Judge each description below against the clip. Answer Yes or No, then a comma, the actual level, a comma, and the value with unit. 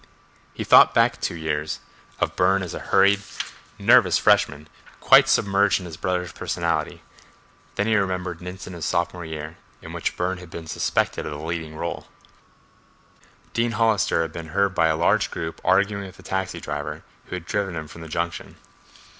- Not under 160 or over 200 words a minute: Yes, average, 180 wpm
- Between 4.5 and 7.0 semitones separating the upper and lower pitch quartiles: No, average, 3.1 semitones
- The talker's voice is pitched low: Yes, very low, 90 Hz